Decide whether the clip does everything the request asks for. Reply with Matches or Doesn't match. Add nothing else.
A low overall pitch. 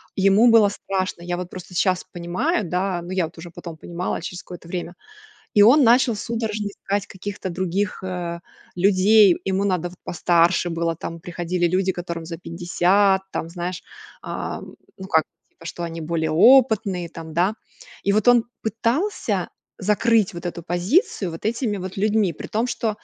Doesn't match